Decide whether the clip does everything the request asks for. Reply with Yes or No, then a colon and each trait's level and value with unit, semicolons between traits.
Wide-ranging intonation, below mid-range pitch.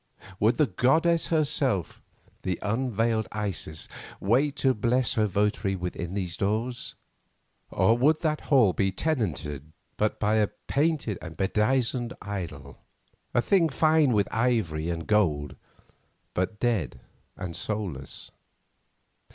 Yes: wide, 5.8 semitones; low, 105 Hz